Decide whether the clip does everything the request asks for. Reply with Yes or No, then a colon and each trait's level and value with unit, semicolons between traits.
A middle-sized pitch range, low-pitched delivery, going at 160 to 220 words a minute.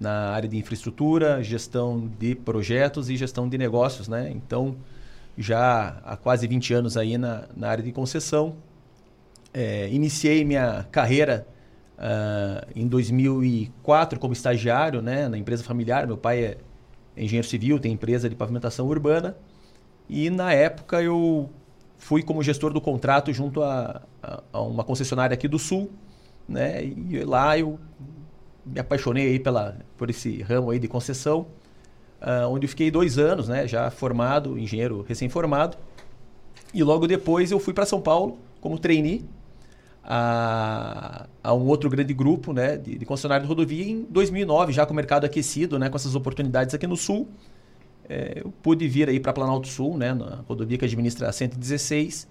Yes: average, 4.0 semitones; low, 130 Hz; average, 165 wpm